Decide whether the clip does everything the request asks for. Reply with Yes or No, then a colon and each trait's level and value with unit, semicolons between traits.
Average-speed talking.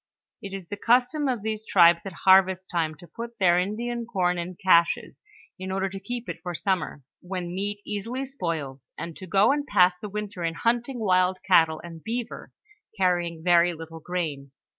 Yes: average, 185 wpm